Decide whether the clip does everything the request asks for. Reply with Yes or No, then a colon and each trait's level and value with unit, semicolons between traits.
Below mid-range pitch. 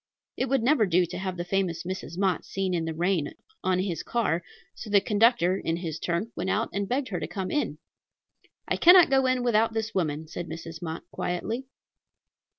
No: high, 190 Hz